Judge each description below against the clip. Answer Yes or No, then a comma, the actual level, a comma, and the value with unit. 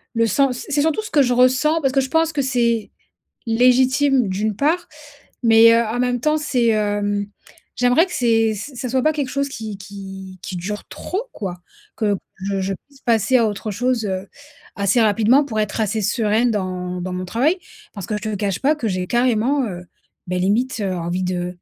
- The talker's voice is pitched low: No, high, 225 Hz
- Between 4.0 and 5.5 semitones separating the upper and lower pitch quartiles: Yes, average, 4.6 semitones